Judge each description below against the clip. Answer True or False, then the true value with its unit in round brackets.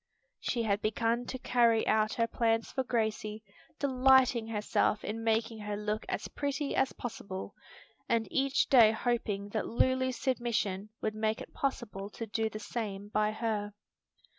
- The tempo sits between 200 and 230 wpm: False (155 wpm)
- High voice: True (225 Hz)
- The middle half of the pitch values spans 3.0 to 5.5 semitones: False (2.4 semitones)